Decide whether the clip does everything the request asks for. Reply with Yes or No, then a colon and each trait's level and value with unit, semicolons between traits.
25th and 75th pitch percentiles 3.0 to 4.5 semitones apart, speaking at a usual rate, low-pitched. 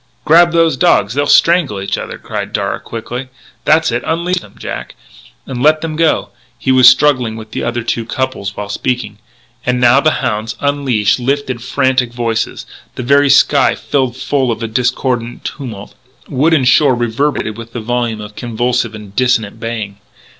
Yes: average, 3.8 semitones; average, 170 wpm; low, 125 Hz